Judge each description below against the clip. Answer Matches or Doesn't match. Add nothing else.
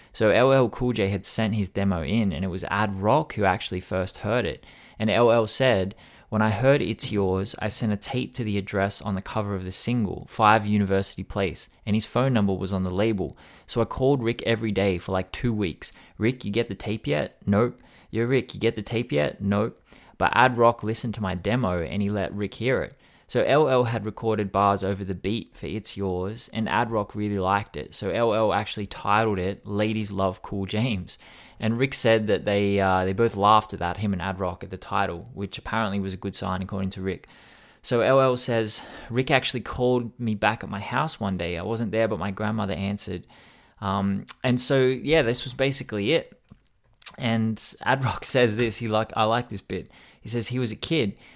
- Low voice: Matches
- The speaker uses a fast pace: Matches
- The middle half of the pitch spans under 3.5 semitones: Matches